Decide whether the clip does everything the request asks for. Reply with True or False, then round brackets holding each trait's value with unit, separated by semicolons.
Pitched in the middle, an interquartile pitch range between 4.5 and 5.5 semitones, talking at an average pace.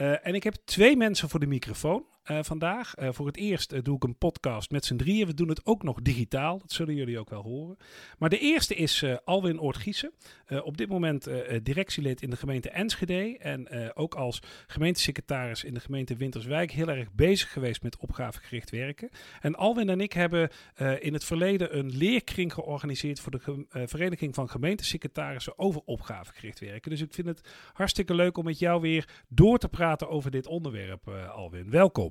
False (150 Hz; 5.2 semitones; 205 wpm)